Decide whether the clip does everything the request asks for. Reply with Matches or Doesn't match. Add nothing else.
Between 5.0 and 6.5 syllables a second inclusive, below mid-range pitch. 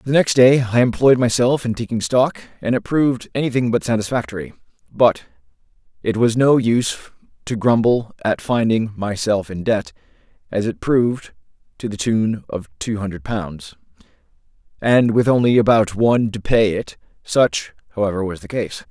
Matches